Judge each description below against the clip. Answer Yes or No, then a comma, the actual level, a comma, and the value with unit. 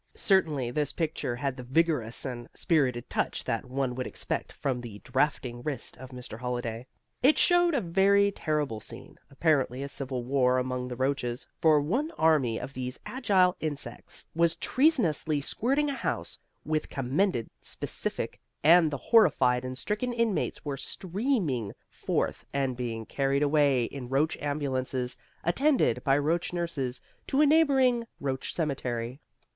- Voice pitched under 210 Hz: Yes, medium, 140 Hz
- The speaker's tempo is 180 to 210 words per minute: No, average, 150 wpm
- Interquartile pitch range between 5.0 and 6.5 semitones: Yes, wide, 5.6 semitones